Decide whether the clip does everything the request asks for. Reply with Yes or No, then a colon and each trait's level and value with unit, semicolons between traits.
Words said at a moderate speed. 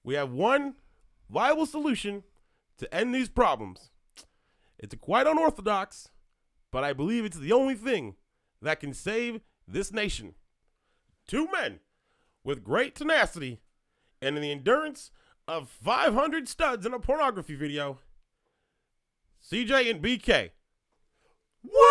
No: slow, 120 wpm